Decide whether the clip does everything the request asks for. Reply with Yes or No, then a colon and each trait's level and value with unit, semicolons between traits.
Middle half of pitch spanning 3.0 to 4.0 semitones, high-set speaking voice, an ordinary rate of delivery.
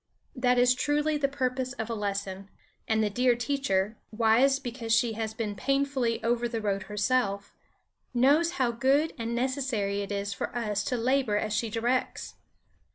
Yes: average, 3.6 semitones; high, 235 Hz; average, 165 wpm